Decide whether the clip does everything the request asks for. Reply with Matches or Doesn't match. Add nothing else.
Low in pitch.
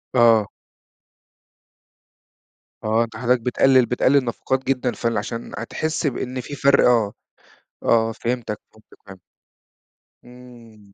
Matches